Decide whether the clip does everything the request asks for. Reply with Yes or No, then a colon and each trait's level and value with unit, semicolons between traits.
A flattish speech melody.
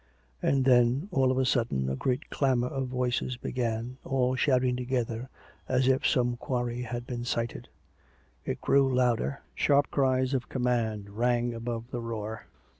Yes: narrow, 1.6 semitones